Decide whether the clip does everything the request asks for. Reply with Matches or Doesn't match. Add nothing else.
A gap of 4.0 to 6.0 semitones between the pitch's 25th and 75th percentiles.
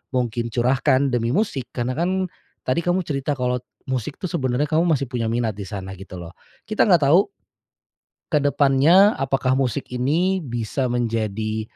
Matches